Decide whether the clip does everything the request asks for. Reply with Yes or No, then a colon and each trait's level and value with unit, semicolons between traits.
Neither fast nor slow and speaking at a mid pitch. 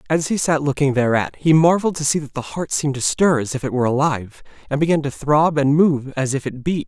No: fast, 260 wpm; medium, 145 Hz